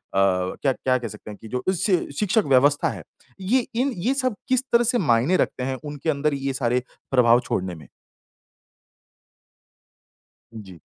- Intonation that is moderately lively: No, wide, 8.1 semitones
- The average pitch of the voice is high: No, low, 135 Hz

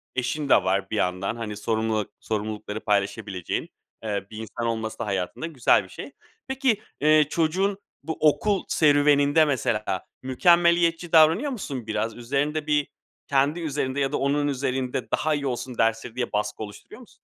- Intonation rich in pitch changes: Yes, wide, 5.9 semitones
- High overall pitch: No, low, 130 Hz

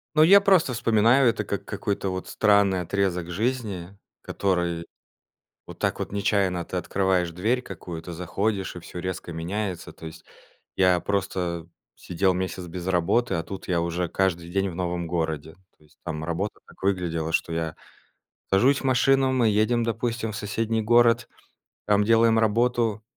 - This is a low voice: Yes, very low, 95 Hz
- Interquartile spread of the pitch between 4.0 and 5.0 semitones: Yes, average, 4.4 semitones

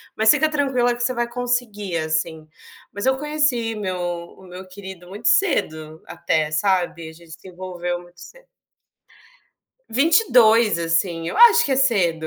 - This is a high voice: Yes, high, 200 Hz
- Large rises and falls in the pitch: Yes, wide, 6.4 semitones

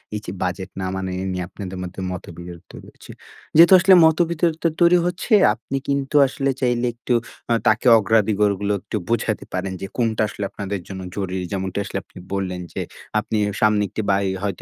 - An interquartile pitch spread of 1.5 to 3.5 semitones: No, average, 4.6 semitones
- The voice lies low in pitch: Yes, low, 105 Hz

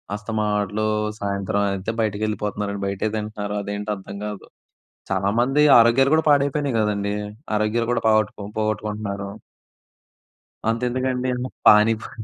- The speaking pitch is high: No, low, 105 Hz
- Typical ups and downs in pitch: No, narrow, 2.3 semitones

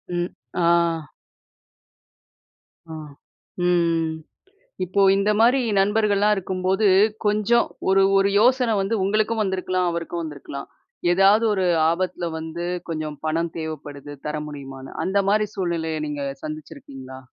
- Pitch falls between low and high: Yes, medium, 180 Hz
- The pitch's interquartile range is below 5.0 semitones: Yes, average, 4.2 semitones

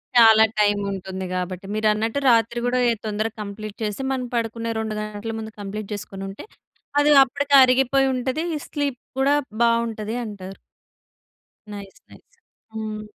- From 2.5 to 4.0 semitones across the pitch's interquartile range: Yes, average, 2.9 semitones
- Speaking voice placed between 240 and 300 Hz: No, high, 220 Hz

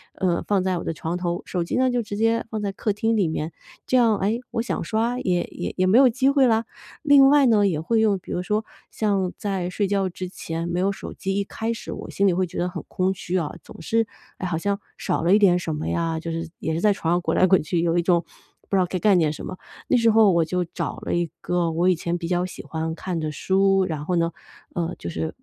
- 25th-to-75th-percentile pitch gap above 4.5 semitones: No, average, 3.8 semitones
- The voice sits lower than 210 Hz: Yes, medium, 185 Hz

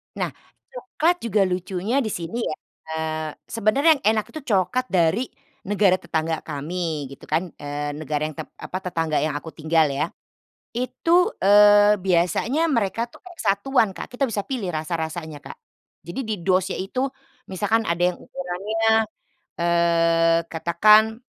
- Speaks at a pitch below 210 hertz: Yes, medium, 185 Hz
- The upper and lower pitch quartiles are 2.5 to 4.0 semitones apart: No, average, 5.3 semitones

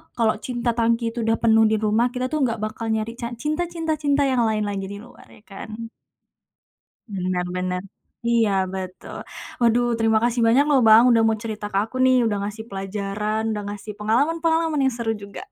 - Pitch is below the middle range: No, high, 225 Hz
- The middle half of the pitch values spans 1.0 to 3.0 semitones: Yes, average, 2.7 semitones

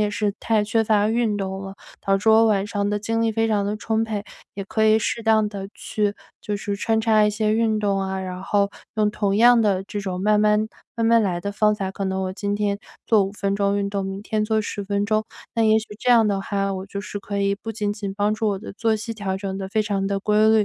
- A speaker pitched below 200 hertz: No, high, 205 Hz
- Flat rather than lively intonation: Yes, narrow, 1.6 semitones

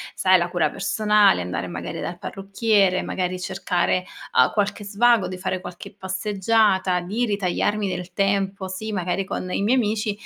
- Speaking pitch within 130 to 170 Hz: No, high, 195 Hz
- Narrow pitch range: Yes, narrow, 2.3 semitones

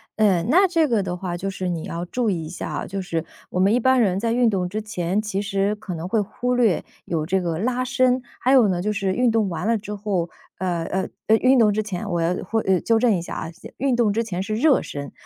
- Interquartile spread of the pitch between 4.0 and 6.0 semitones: Yes, average, 4.3 semitones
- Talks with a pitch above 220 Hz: No, high, 205 Hz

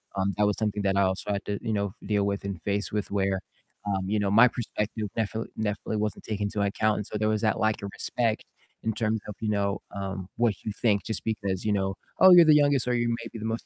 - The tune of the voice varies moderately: No, narrow, 1.8 semitones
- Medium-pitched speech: No, low, 105 Hz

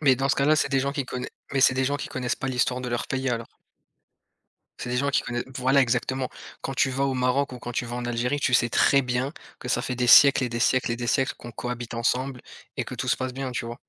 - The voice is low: Yes, low, 125 Hz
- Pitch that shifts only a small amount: Yes, narrow, 1.7 semitones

